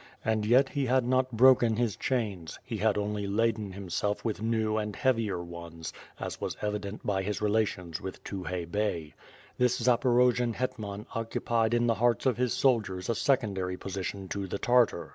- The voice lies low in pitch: Yes, low, 110 Hz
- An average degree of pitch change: Yes, average, 3.4 semitones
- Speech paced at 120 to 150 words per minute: No, average, 170 wpm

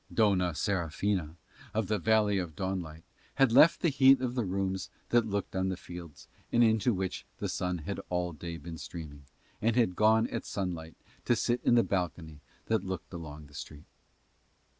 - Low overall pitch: Yes, very low, 95 Hz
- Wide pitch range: No, average, 4.8 semitones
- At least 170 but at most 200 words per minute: Yes, average, 180 wpm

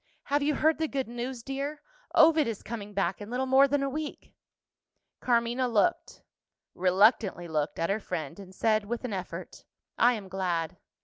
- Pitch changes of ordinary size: No, wide, 5.8 semitones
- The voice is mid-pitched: No, high, 235 Hz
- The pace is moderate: Yes, average, 175 wpm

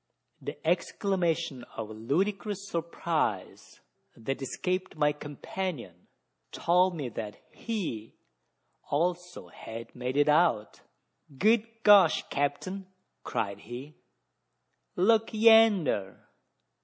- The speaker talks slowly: Yes, slow, 90 wpm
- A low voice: No, medium, 170 Hz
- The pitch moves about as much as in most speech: No, wide, 6.9 semitones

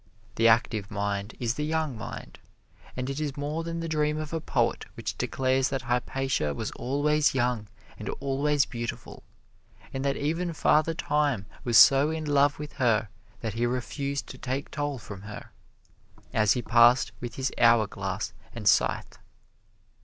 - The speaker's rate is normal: Yes, average, 160 wpm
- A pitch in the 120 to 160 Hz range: Yes, low, 135 Hz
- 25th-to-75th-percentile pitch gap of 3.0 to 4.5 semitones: Yes, average, 4.1 semitones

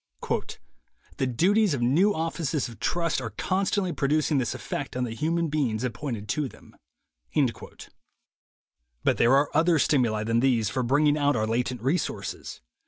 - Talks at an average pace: Yes, average, 155 wpm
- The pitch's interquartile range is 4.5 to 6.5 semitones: Yes, average, 5.2 semitones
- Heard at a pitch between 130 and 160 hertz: Yes, medium, 140 Hz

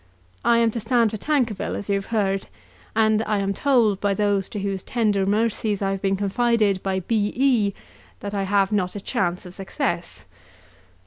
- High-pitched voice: Yes, high, 205 Hz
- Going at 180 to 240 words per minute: Yes, average, 190 wpm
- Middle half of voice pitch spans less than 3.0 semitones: Yes, narrow, 2.5 semitones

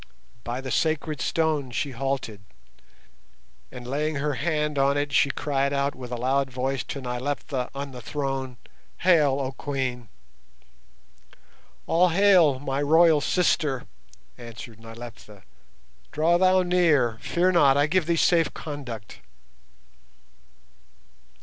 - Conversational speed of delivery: No, slow, 125 wpm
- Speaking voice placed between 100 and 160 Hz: Yes, medium, 140 Hz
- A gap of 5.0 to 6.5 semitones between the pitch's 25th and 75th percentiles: No, average, 3.5 semitones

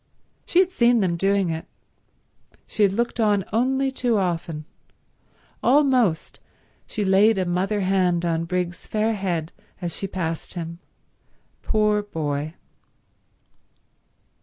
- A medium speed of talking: No, slow, 120 wpm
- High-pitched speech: Yes, high, 195 Hz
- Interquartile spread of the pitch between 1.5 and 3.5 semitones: No, average, 4.3 semitones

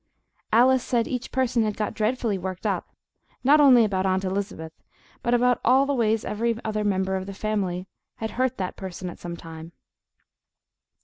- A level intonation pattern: No, average, 4.4 semitones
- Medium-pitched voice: No, high, 215 Hz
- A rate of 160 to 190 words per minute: Yes, average, 175 wpm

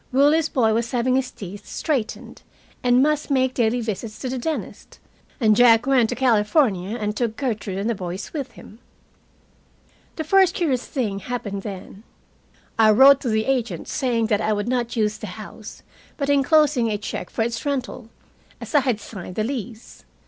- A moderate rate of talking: Yes, average, 180 wpm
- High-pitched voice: Yes, high, 240 Hz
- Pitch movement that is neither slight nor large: Yes, average, 3.8 semitones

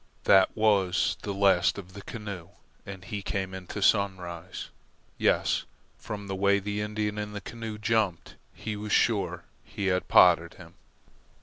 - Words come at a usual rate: Yes, average, 160 wpm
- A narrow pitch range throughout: Yes, narrow, 1.8 semitones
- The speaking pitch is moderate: No, low, 100 Hz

